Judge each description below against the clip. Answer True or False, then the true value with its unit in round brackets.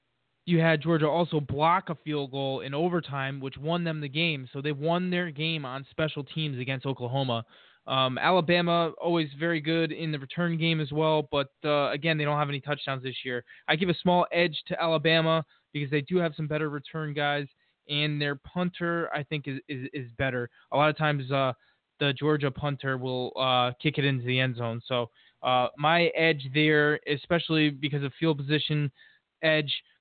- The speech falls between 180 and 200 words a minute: True (195 wpm)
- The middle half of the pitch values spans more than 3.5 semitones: False (3.0 semitones)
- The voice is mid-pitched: True (150 Hz)